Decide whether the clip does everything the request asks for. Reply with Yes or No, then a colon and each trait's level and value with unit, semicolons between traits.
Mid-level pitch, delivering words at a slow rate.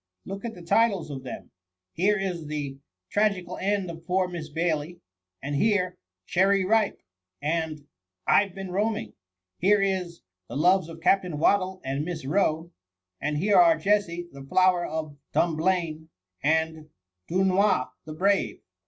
No: medium, 170 Hz; average, 170 wpm